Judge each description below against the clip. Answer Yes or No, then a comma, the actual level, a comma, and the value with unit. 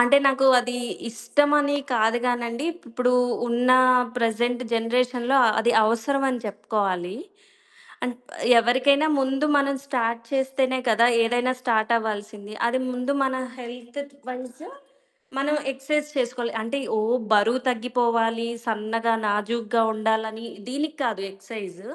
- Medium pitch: No, high, 240 Hz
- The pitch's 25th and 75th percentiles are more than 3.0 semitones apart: No, narrow, 2.5 semitones